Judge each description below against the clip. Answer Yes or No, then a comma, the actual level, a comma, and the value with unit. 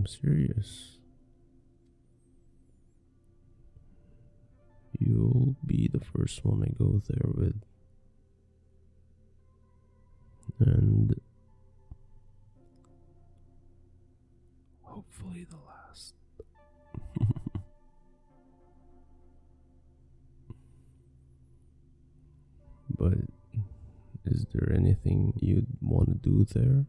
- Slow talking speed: Yes, slow, 50 wpm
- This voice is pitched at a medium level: No, low, 100 Hz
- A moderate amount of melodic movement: No, wide, 5.9 semitones